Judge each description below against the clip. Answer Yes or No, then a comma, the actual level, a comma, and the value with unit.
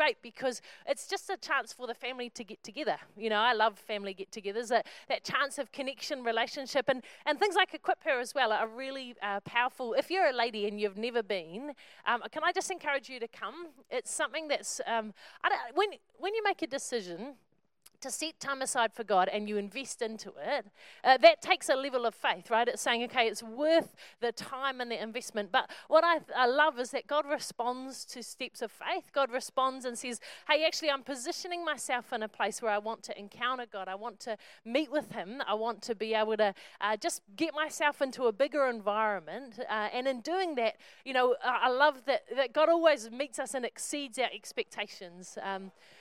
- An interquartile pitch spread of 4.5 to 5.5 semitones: Yes, average, 4.8 semitones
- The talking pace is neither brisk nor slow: No, fast, 215 wpm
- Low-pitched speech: No, very high, 250 Hz